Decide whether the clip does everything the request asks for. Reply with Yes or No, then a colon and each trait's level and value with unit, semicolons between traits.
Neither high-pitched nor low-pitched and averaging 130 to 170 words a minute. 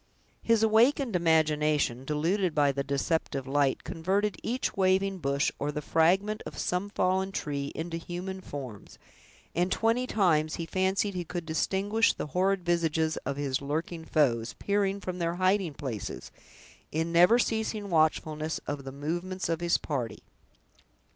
Yes: medium, 170 Hz; average, 145 wpm